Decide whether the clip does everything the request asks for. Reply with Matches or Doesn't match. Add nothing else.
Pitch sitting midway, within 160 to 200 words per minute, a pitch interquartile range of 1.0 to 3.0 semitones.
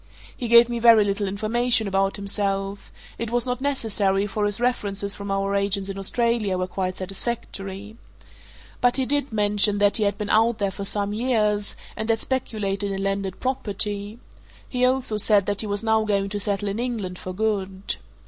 Doesn't match